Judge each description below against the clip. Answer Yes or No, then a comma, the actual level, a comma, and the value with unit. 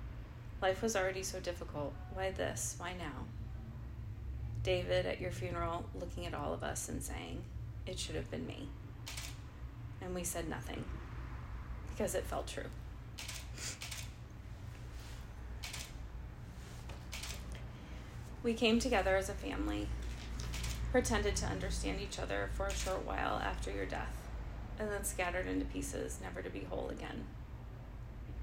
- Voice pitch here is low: Yes, very low, 90 Hz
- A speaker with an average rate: No, slow, 130 wpm